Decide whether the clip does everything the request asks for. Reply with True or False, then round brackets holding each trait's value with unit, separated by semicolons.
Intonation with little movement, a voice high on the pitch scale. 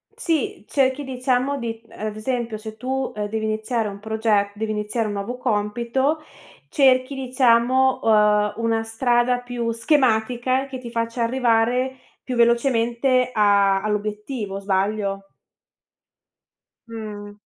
False (3.1 semitones; 230 Hz)